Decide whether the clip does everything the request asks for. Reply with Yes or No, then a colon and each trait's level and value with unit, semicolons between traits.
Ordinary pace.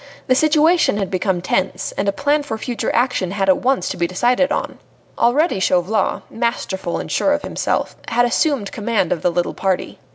Yes: average, 190 wpm